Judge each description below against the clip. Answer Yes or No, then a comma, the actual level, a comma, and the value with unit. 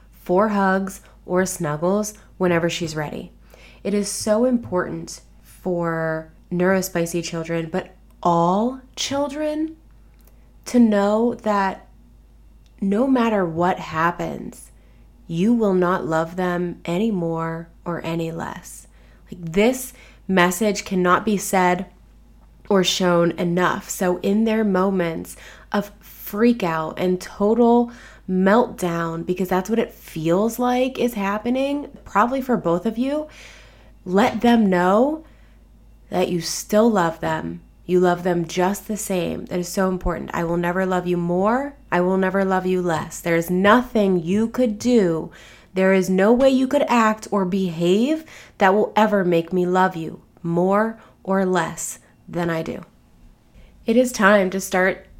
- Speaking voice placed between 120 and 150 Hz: No, high, 190 Hz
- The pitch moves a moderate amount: Yes, average, 3.8 semitones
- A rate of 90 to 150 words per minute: Yes, average, 140 wpm